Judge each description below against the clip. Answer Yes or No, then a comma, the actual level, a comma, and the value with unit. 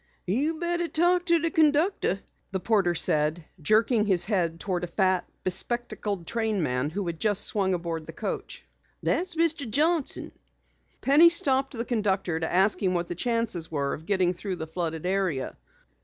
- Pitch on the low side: No, high, 195 Hz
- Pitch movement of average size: No, wide, 7.6 semitones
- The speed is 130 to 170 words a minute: Yes, average, 165 wpm